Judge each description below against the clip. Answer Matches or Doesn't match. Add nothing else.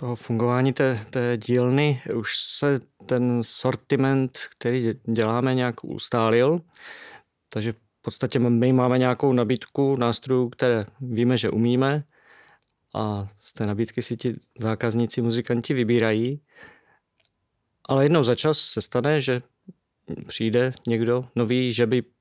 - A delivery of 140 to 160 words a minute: Doesn't match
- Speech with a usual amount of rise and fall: Doesn't match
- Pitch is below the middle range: Matches